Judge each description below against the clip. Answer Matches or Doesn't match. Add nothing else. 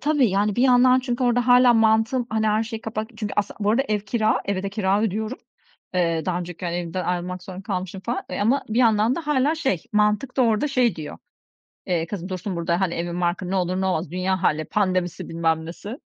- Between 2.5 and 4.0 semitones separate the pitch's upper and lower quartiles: Doesn't match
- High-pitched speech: Matches